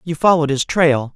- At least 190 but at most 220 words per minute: Yes, fast, 210 wpm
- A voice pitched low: No, medium, 155 Hz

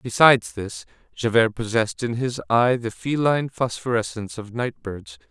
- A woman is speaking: No, male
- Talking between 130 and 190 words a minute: Yes, average, 145 wpm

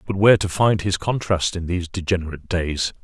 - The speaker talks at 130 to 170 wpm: No, average, 200 wpm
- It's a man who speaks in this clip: Yes, male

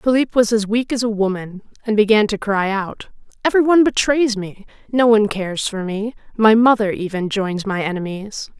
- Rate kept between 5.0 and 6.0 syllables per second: Yes, 5.3 syllables/s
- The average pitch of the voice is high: Yes, high, 215 Hz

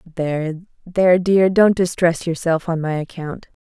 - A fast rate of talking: No, average, 150 wpm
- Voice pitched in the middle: Yes, medium, 170 Hz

